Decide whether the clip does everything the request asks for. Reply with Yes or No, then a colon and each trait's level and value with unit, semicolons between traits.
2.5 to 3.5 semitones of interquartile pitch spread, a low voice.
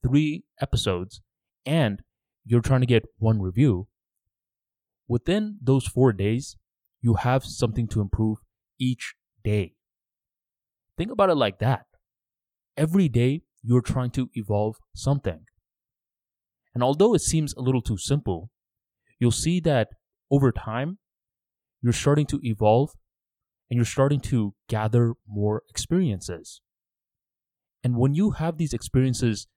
No: average, 4.1 semitones; low, 120 Hz